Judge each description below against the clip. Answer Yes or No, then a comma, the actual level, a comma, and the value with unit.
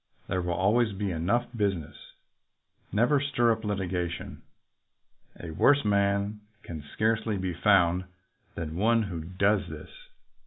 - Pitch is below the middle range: Yes, low, 100 Hz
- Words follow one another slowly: Yes, slow, 125 wpm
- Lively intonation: No, average, 3.9 semitones